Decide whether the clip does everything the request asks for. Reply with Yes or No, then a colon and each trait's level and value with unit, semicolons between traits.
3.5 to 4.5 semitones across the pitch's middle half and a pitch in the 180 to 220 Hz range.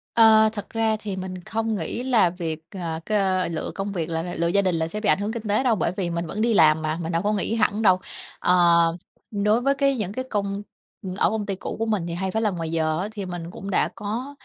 Yes: average, 4.2 semitones; high, 200 Hz